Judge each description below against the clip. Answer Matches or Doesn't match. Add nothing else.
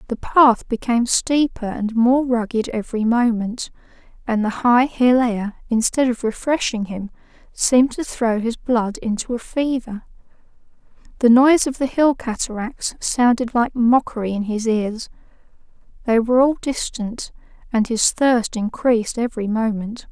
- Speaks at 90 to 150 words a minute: Matches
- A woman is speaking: Matches